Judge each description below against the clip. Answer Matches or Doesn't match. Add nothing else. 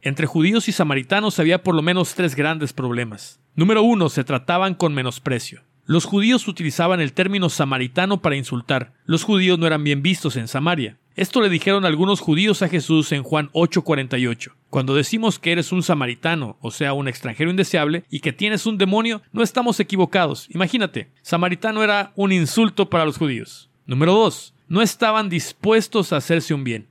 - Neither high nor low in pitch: Matches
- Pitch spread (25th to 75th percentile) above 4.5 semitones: Matches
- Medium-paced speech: Matches